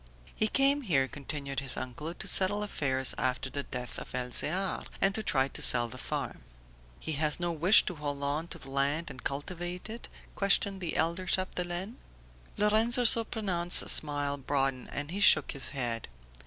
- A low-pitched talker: No, medium, 155 Hz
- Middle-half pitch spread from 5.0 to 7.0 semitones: Yes, wide, 5.6 semitones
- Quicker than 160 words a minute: Yes, average, 170 wpm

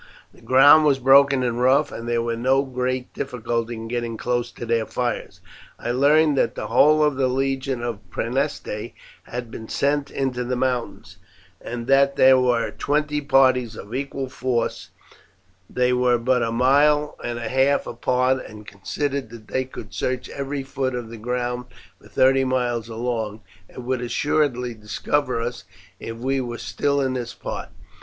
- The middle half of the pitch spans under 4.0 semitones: Yes, narrow, 2.4 semitones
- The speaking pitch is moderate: No, low, 125 Hz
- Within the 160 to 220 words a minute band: Yes, average, 170 wpm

